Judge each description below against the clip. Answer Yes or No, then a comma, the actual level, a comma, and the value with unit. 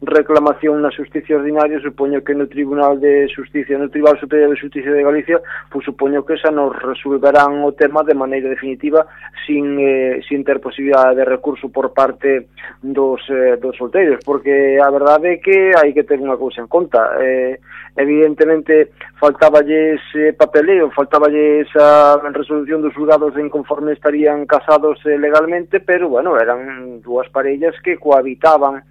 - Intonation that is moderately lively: No, narrow, 1.7 semitones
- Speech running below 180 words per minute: Yes, average, 160 wpm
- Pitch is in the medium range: Yes, medium, 145 Hz